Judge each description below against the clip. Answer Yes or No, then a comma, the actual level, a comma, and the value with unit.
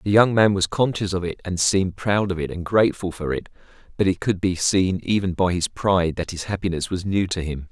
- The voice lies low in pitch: Yes, very low, 95 Hz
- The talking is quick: Yes, fast, 250 wpm